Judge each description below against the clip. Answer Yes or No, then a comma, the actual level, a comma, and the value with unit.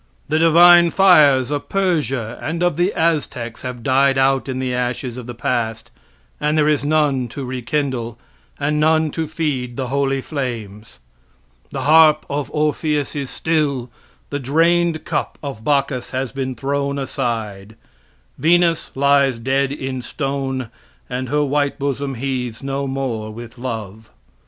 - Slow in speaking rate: No, average, 145 wpm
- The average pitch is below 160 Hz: Yes, low, 135 Hz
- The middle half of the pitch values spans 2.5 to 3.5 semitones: Yes, average, 3.2 semitones